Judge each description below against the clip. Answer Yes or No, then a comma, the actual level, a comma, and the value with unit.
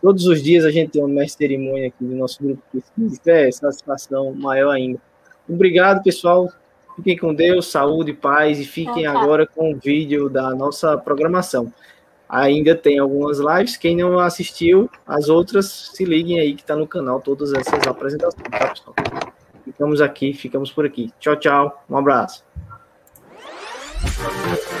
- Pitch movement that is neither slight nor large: Yes, average, 3.8 semitones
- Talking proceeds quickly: No, average, 150 wpm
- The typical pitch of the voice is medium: Yes, medium, 150 Hz